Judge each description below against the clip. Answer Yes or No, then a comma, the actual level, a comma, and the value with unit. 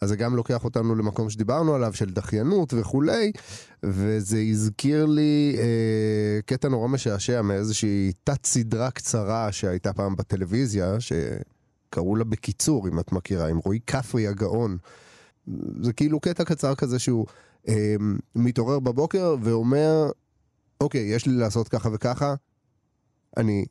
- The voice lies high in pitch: No, low, 115 Hz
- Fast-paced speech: No, average, 130 wpm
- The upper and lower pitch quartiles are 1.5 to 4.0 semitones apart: No, average, 4.4 semitones